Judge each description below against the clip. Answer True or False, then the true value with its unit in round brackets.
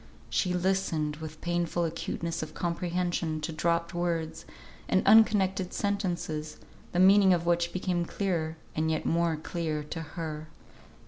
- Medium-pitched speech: True (170 Hz)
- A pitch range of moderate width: False (2.2 semitones)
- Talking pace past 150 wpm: False (135 wpm)